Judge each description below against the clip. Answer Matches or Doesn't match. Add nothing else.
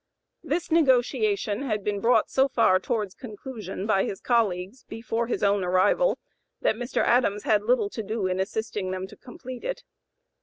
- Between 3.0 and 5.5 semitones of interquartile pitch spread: Matches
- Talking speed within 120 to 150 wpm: Doesn't match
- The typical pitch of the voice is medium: Doesn't match